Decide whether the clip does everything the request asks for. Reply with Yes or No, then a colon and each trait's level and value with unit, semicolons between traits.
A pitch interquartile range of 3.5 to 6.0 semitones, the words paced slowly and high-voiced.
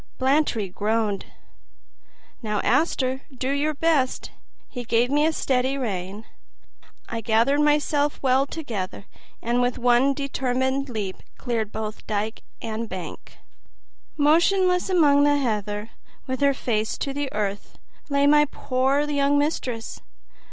Yes: average, 4.5 semitones; slow, 125 wpm; very high, 260 Hz